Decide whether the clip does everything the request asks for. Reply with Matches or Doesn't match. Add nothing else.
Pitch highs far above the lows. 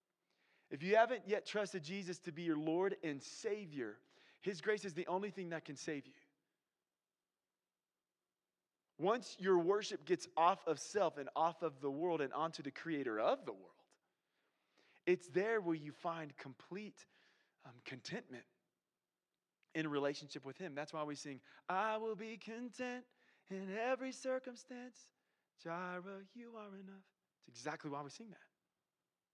Matches